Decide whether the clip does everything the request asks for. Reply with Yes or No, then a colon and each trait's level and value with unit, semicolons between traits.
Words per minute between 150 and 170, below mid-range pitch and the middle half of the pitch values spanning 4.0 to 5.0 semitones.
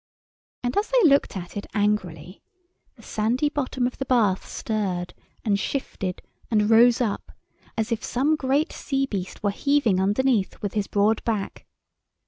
No: average, 155 wpm; high, 220 Hz; average, 4.7 semitones